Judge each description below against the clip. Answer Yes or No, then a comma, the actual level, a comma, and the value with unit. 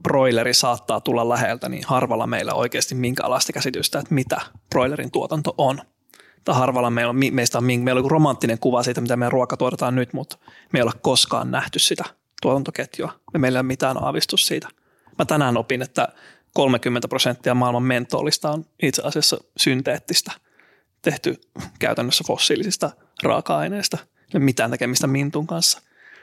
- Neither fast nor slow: No, fast, 160 wpm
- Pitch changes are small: Yes, narrow, 2.0 semitones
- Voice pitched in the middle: No, low, 130 Hz